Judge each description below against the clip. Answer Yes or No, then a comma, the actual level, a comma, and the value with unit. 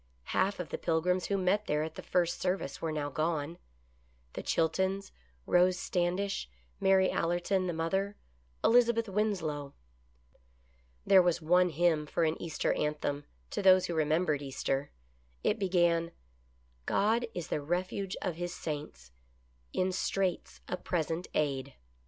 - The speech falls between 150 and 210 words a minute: No, average, 140 wpm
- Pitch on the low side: No, medium, 175 Hz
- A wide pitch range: No, average, 3.5 semitones